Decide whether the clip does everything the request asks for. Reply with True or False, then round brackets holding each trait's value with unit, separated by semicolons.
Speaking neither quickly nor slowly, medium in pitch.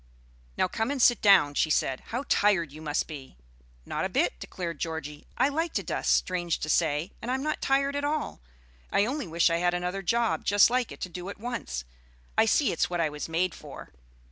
False (220 wpm; 180 Hz)